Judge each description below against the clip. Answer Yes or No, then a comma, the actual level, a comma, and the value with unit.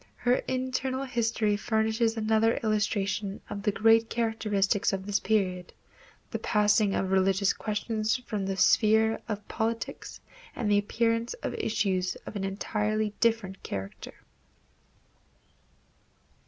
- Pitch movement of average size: No, narrow, 2.3 semitones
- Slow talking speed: Yes, slow, 120 wpm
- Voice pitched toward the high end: Yes, high, 215 Hz